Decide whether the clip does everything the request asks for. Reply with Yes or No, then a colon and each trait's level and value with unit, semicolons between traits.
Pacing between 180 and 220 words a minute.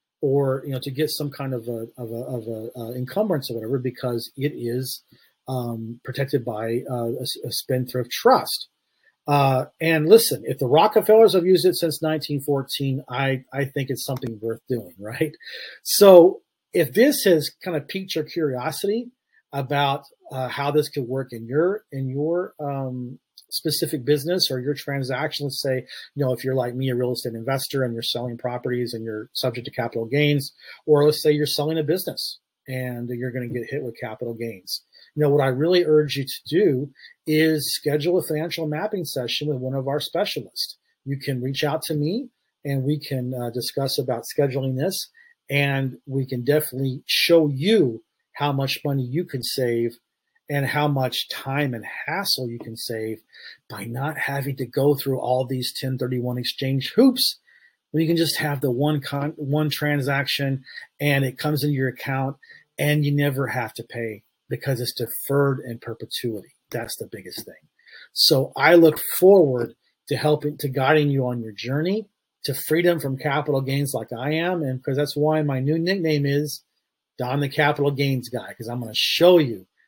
Yes: average, 185 wpm